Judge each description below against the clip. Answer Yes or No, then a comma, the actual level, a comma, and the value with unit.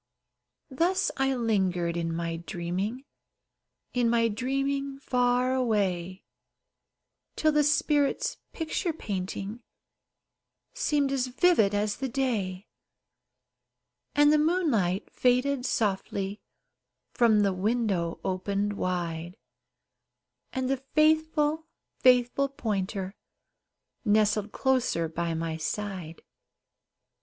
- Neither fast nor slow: No, slow, 95 wpm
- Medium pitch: No, high, 230 Hz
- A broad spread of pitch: Yes, wide, 6.4 semitones